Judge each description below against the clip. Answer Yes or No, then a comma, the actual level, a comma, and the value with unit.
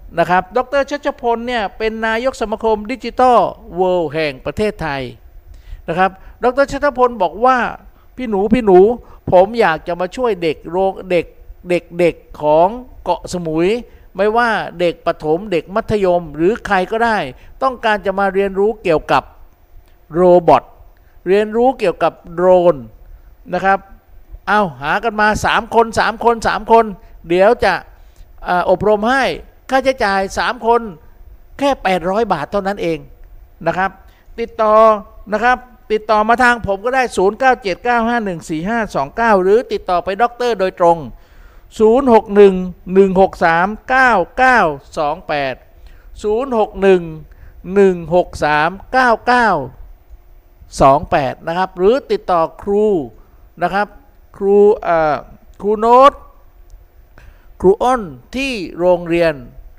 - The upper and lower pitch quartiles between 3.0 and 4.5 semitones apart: No, average, 5.3 semitones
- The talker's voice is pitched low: No, high, 195 Hz